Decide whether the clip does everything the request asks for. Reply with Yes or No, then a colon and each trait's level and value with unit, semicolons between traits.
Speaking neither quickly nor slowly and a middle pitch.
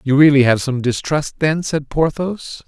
Yes: average, 180 wpm; medium, 145 Hz